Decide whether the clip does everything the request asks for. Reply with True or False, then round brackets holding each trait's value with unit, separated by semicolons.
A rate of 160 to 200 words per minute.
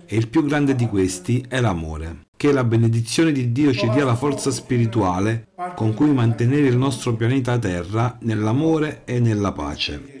True (170 wpm)